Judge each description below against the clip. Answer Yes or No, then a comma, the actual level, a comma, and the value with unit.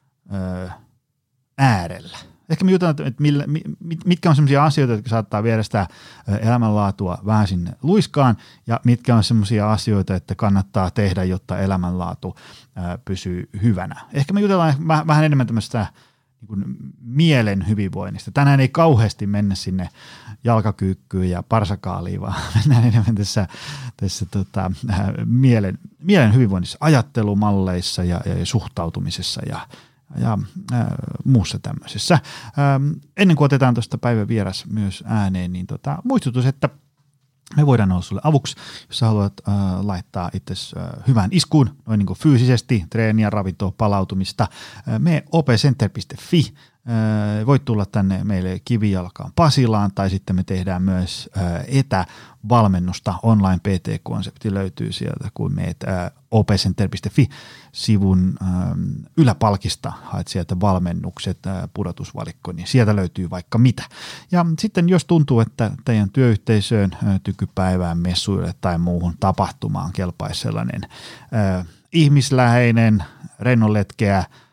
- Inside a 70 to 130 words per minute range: Yes, average, 120 wpm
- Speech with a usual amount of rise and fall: No, wide, 5.7 semitones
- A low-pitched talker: Yes, low, 110 Hz